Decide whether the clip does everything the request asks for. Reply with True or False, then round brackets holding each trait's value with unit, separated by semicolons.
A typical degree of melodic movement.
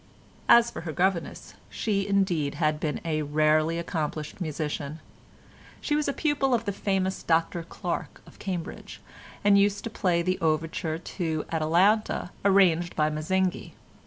True (4.0 semitones)